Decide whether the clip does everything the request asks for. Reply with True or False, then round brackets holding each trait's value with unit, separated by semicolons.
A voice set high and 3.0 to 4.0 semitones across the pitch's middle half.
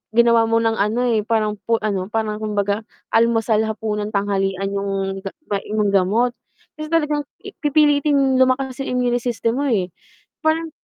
True (225 Hz; 3.7 semitones)